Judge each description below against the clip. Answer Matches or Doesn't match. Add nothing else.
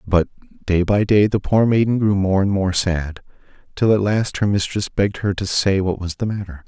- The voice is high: Doesn't match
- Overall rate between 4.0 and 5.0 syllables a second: Doesn't match